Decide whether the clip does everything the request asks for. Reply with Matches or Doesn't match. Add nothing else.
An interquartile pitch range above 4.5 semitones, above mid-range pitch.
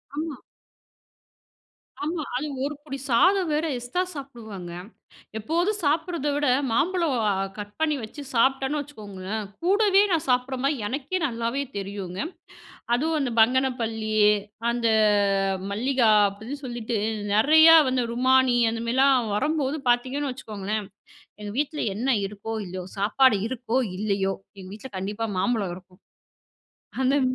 Matches